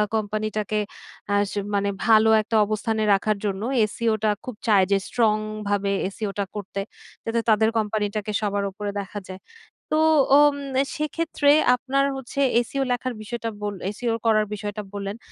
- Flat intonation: Yes, narrow, 2.1 semitones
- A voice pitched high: Yes, high, 215 Hz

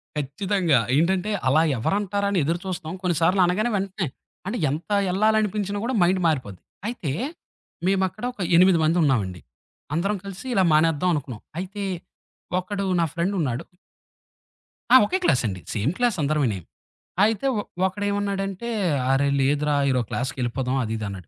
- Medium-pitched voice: Yes, medium, 175 Hz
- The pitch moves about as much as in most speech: No, wide, 6.2 semitones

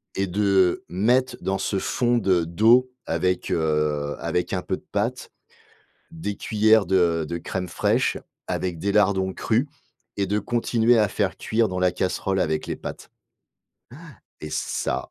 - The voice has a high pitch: No, very low, 95 Hz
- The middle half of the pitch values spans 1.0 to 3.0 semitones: No, average, 3.7 semitones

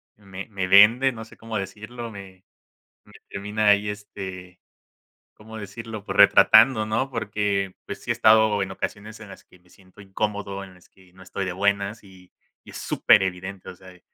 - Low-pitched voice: Yes, low, 100 Hz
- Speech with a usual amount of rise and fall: No, narrow, 2.3 semitones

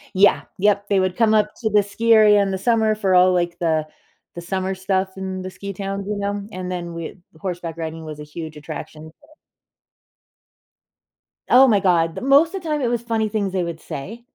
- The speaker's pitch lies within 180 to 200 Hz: Yes, high, 190 Hz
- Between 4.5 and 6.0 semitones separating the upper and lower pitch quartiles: No, average, 3.7 semitones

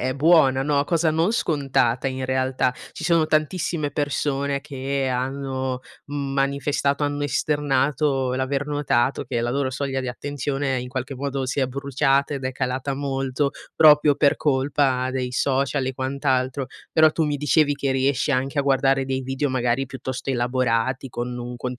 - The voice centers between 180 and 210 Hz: No, low, 135 Hz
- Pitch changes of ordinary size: No, narrow, 1.7 semitones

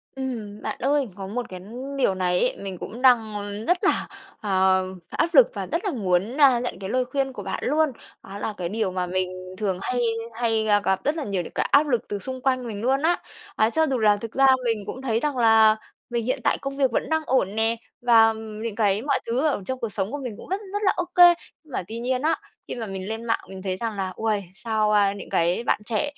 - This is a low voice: No, high, 225 Hz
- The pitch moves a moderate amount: Yes, average, 4.5 semitones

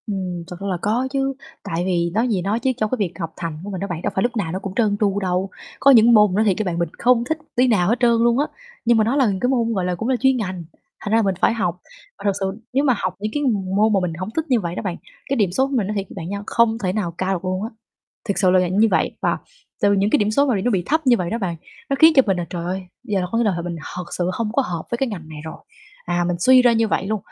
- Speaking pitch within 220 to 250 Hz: No, high, 205 Hz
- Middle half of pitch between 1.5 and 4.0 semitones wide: No, average, 4.4 semitones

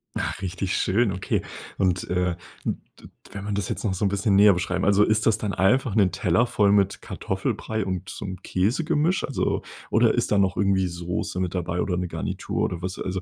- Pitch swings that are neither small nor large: No, narrow, 2.2 semitones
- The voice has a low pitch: Yes, very low, 95 Hz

